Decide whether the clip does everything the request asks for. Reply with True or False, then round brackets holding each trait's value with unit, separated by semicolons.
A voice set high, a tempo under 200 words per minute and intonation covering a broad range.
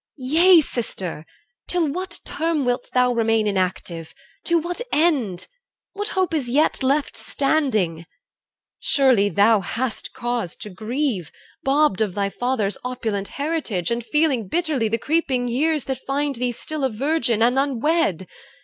True (250 Hz; 140 wpm; 5.9 semitones)